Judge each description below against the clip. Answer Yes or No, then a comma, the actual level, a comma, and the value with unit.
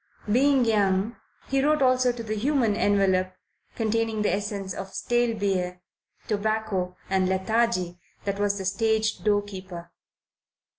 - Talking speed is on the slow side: Yes, slow, 130 wpm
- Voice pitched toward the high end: Yes, high, 205 Hz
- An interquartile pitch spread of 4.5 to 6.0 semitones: No, average, 3.1 semitones